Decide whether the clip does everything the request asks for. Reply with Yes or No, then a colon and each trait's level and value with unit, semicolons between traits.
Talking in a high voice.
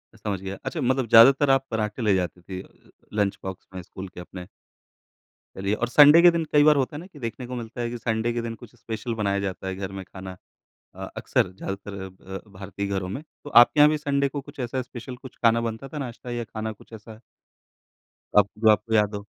No: low, 110 Hz